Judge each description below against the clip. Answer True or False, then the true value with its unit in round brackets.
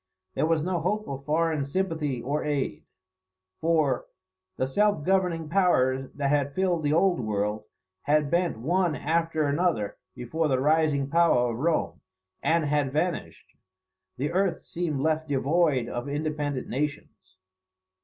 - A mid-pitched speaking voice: True (150 Hz)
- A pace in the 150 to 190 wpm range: False (140 wpm)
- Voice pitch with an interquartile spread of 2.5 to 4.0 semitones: True (3.5 semitones)